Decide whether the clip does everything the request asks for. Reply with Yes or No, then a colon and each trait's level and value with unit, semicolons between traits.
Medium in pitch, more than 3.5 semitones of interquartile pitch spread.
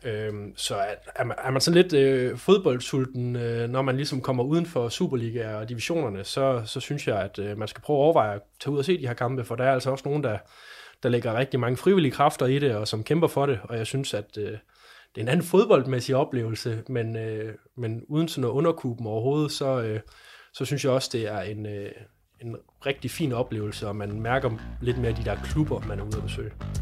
No: low, 125 Hz; average, 4.1 semitones